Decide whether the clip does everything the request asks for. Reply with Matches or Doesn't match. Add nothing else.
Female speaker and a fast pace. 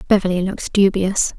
Doesn't match